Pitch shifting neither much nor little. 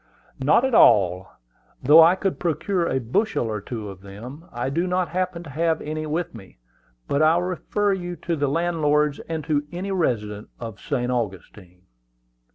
No: wide, 6.9 semitones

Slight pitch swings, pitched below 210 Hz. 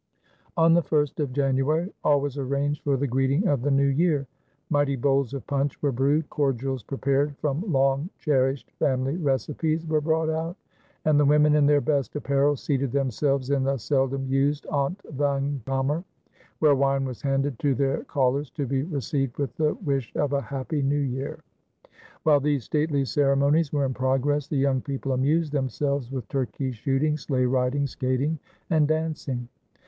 Yes: narrow, 1.8 semitones; medium, 140 Hz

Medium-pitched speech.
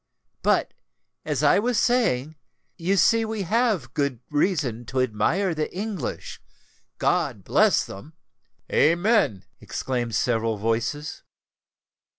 Yes: medium, 150 Hz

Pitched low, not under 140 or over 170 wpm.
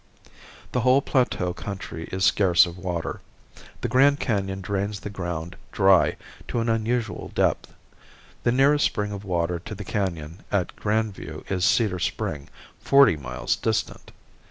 Yes: low, 100 Hz; average, 150 wpm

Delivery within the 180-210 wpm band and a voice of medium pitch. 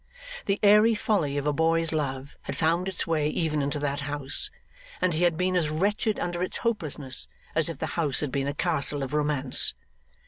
Yes: average, 200 wpm; medium, 155 Hz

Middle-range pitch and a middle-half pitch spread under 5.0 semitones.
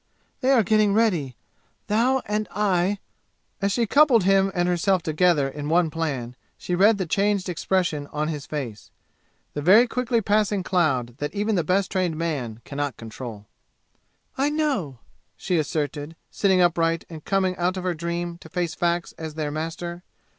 Yes: medium, 175 Hz; average, 4.6 semitones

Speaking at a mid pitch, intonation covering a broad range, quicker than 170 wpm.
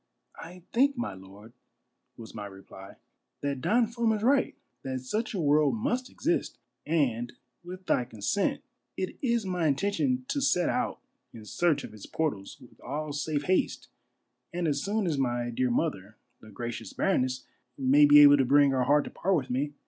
Yes: medium, 145 Hz; wide, 7.8 semitones; average, 185 wpm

